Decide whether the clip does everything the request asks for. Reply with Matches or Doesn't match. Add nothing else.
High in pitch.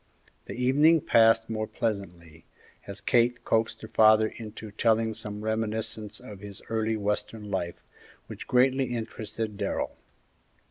Doesn't match